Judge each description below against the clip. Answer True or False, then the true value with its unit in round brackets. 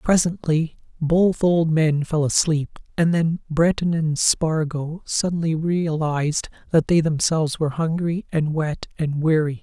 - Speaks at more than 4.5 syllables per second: False (4.2 syllables/s)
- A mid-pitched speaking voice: True (160 Hz)